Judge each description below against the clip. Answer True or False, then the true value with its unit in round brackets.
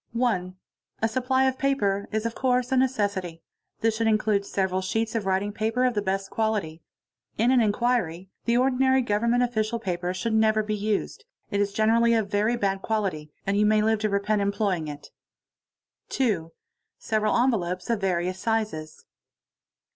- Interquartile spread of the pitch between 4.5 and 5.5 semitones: False (3.2 semitones)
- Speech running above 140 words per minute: True (170 wpm)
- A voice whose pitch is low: False (215 Hz)